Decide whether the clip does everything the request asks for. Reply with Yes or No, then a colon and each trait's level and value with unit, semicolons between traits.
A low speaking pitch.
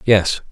Yes: very low, 95 Hz